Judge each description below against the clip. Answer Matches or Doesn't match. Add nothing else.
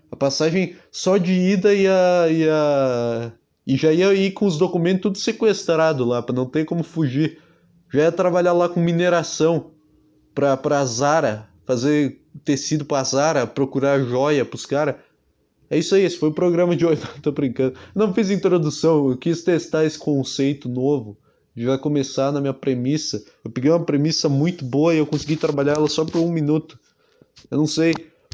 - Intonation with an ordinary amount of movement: Matches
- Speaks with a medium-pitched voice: Matches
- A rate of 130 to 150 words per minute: Doesn't match